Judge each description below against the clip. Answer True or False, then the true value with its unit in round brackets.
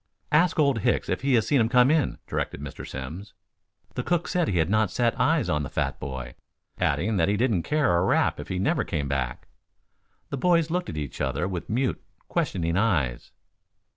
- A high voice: False (100 Hz)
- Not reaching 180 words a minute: False (200 wpm)